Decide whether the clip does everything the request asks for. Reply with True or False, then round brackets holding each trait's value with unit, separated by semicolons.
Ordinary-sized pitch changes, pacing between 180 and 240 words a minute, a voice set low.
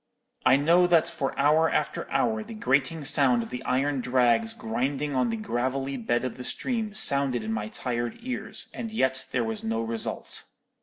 True (4.2 semitones; 185 wpm; 130 Hz)